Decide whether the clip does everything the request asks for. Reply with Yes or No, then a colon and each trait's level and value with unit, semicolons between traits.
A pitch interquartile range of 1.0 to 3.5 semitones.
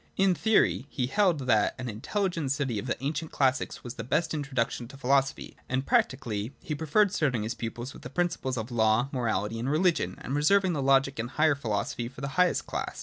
No: average, 4.6 semitones